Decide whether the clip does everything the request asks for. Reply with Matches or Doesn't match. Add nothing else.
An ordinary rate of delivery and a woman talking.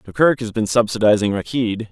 Doesn't match